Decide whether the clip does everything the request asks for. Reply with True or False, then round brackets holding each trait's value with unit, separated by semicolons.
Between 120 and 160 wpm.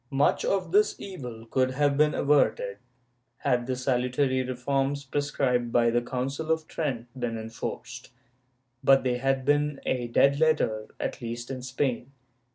True (155 wpm)